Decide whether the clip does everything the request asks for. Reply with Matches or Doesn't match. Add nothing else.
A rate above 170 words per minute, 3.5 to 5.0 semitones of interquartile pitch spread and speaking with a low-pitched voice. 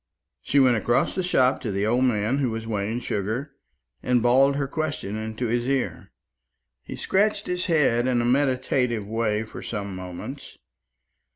Doesn't match